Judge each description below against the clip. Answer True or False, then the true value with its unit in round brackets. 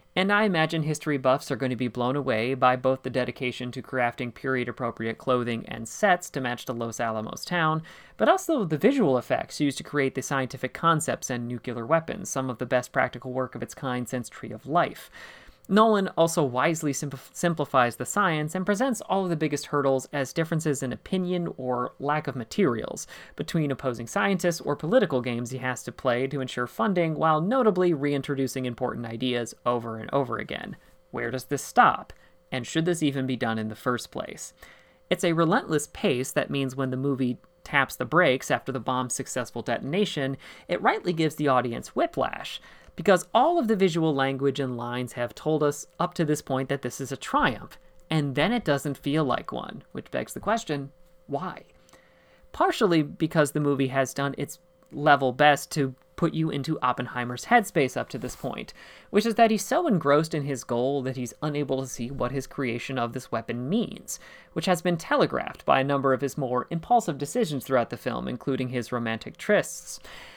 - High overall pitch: False (135 Hz)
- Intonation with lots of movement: False (4.4 semitones)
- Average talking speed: True (195 wpm)